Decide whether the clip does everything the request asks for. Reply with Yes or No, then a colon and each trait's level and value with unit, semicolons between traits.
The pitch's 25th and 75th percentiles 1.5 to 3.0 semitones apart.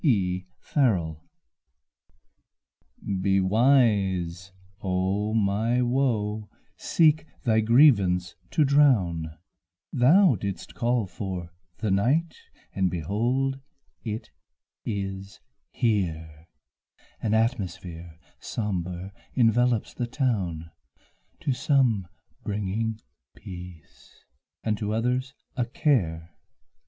No: average, 5.0 semitones